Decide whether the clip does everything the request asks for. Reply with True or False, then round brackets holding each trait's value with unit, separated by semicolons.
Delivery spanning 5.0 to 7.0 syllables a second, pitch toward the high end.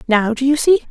True (5.5 syllables/s; 260 Hz)